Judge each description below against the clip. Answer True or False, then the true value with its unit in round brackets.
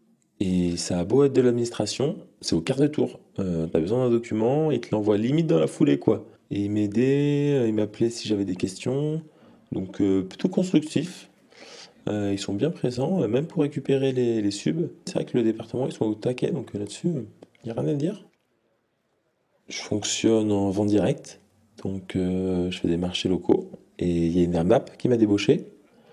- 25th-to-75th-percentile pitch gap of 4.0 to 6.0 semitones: True (5.4 semitones)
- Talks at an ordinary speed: True (200 wpm)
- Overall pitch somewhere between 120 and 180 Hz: False (110 Hz)